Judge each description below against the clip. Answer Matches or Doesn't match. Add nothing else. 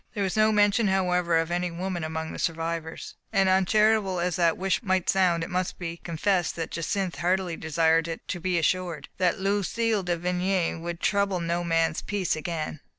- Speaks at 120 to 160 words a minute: Doesn't match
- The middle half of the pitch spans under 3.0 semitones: Matches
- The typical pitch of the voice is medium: Matches